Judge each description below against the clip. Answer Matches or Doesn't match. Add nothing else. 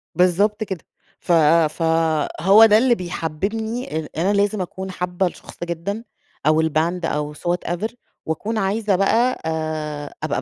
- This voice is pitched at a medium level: Matches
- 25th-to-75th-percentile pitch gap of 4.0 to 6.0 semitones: Matches